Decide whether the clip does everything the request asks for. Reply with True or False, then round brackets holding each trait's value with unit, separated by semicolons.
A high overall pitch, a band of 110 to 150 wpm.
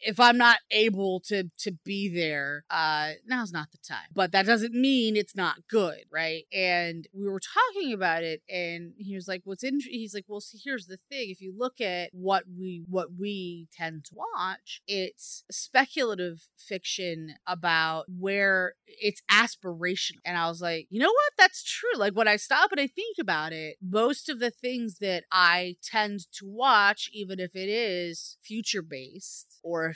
False (195 Hz; 185 wpm)